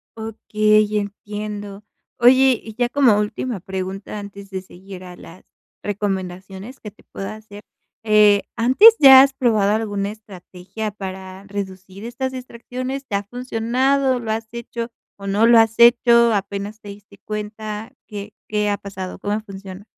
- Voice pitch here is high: Yes, high, 210 Hz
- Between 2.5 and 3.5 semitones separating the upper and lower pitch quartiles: Yes, average, 2.9 semitones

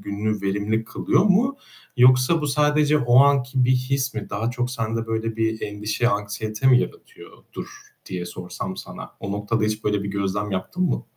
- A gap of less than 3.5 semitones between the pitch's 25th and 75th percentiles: No, average, 4.1 semitones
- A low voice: Yes, low, 115 Hz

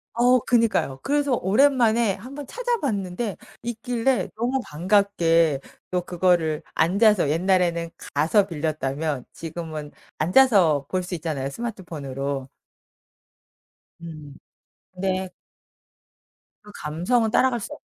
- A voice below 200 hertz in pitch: Yes, medium, 185 Hz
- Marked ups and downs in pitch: Yes, wide, 6.6 semitones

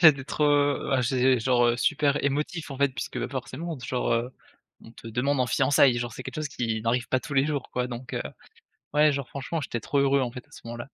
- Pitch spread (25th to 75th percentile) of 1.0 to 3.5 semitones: Yes, narrow, 2.6 semitones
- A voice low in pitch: Yes, low, 130 Hz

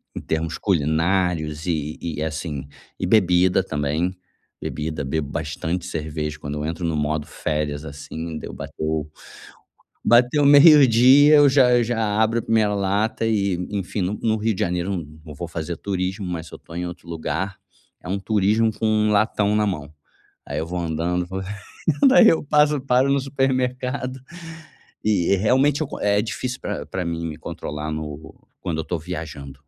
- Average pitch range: No, wide, 5.9 semitones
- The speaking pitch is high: No, very low, 90 Hz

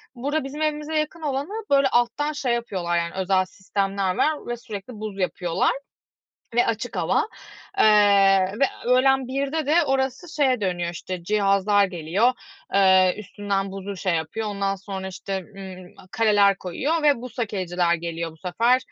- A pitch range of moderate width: No, wide, 5.9 semitones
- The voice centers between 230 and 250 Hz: No, high, 205 Hz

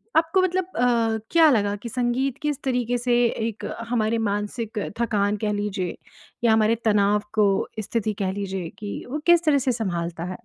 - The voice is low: No, high, 225 Hz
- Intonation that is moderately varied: Yes, average, 3.3 semitones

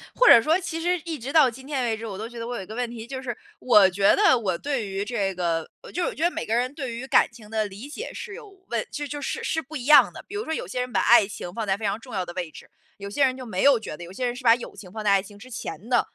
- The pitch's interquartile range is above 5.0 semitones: Yes, wide, 5.4 semitones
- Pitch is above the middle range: Yes, high, 240 Hz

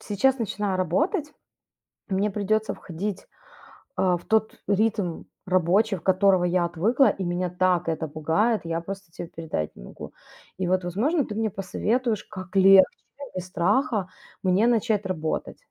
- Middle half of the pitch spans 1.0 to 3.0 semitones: No, average, 3.5 semitones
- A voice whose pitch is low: No, high, 190 Hz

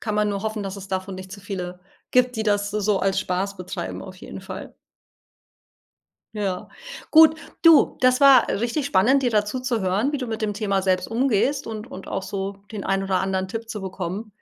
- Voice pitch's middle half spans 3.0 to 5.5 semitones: Yes, average, 3.4 semitones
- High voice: Yes, high, 205 Hz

